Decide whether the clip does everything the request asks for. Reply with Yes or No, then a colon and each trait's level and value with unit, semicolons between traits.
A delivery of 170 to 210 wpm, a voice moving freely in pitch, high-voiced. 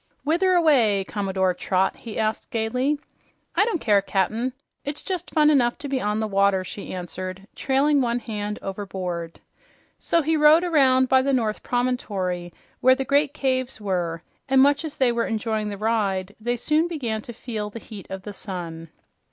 Yes: average, 175 wpm; wide, 5.7 semitones; high, 225 Hz